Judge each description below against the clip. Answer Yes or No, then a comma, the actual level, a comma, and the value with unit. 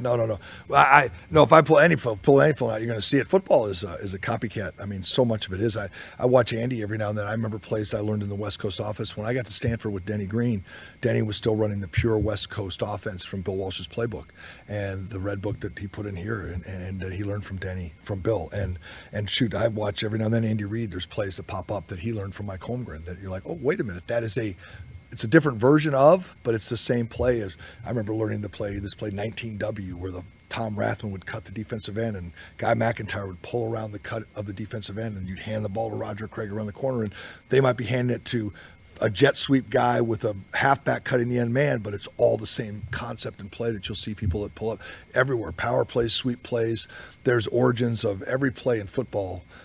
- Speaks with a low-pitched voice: Yes, low, 110 Hz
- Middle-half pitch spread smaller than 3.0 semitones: Yes, narrow, 2.6 semitones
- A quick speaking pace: Yes, fast, 260 wpm